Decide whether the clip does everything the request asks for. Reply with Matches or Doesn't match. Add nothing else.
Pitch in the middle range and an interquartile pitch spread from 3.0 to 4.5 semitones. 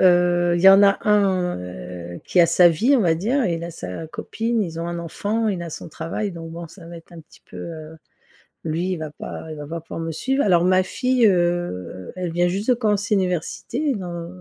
Matches